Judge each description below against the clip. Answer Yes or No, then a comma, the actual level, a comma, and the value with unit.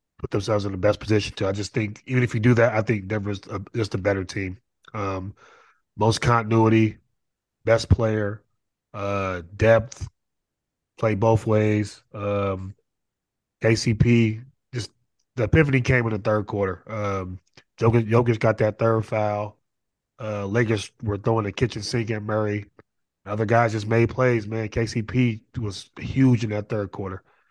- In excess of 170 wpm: No, average, 160 wpm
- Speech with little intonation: Yes, narrow, 2.1 semitones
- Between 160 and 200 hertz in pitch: No, low, 110 Hz